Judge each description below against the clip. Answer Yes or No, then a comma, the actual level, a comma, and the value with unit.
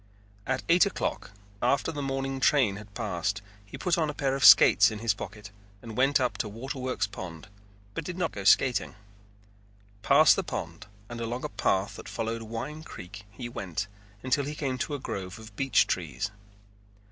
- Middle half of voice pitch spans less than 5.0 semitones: No, average, 5.3 semitones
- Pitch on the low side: Yes, low, 115 Hz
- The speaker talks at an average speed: Yes, average, 180 wpm